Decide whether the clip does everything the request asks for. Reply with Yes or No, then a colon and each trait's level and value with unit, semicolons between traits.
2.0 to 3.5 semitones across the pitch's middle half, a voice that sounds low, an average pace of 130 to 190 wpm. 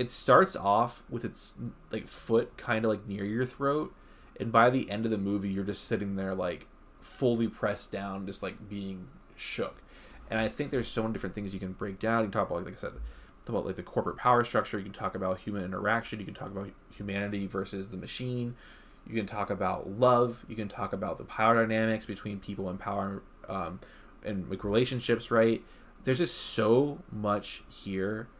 No: average, 2.8 semitones; low, 105 Hz; fast, 205 wpm